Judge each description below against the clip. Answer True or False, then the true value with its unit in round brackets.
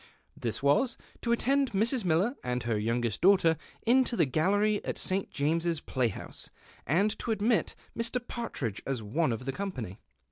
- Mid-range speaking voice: True (170 Hz)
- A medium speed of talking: True (170 wpm)